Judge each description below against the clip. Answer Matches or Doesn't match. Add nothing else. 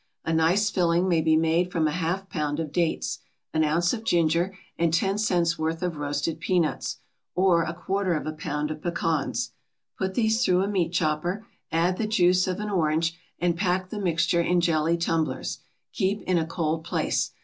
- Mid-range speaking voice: Matches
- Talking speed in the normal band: Matches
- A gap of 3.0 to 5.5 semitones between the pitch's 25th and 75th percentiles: Doesn't match